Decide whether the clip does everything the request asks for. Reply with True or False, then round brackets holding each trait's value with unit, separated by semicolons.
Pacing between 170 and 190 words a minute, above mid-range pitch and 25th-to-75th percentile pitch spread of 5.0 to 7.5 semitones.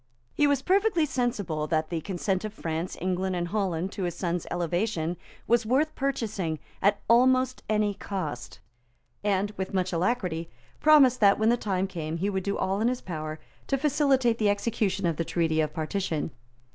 True (175 wpm; 195 Hz; 5.5 semitones)